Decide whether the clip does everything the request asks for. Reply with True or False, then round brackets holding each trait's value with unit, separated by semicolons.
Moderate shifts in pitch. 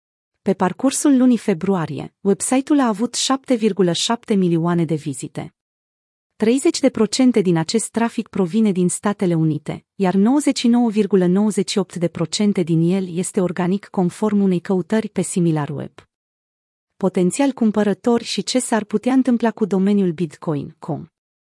True (4.5 semitones)